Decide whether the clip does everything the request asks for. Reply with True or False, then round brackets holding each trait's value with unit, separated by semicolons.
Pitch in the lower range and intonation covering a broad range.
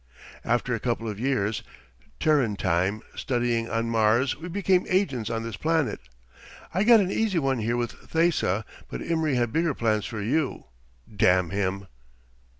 True (120 Hz; 6.7 semitones)